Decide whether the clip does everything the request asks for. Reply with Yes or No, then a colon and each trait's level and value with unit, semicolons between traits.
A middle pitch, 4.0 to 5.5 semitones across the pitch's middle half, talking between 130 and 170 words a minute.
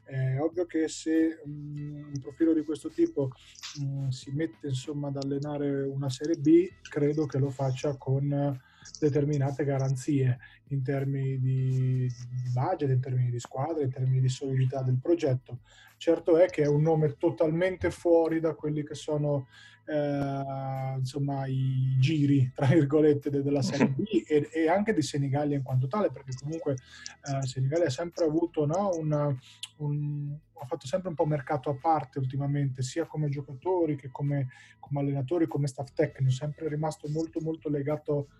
No: medium, 145 Hz; narrow, 2.4 semitones; average, 155 wpm